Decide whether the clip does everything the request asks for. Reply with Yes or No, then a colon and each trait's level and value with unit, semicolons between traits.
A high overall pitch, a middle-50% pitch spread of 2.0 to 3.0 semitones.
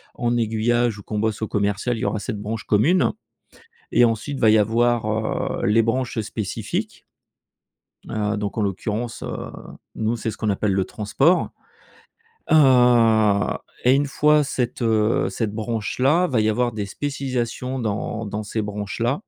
No: low, 110 Hz; narrow, 2.6 semitones